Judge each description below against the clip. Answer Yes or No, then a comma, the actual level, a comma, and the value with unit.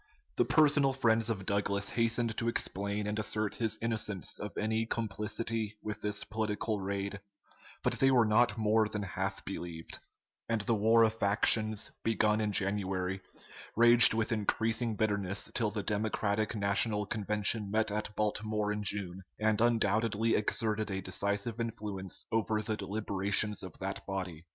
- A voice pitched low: Yes, low, 105 Hz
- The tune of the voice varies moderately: No, narrow, 1.8 semitones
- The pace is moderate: Yes, average, 150 wpm